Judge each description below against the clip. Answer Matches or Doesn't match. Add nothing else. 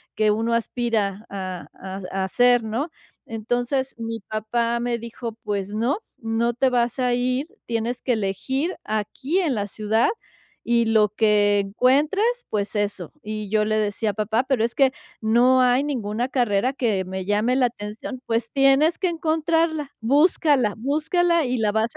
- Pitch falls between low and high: Doesn't match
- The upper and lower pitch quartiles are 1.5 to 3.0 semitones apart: Doesn't match